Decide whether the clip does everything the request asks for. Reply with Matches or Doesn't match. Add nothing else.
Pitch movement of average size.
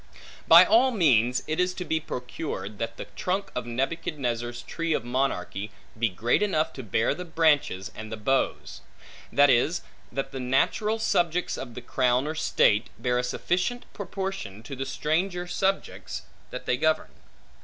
Doesn't match